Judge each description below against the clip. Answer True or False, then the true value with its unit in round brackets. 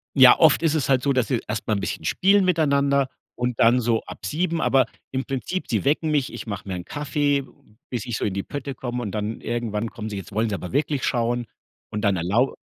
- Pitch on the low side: True (125 Hz)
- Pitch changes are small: False (4.4 semitones)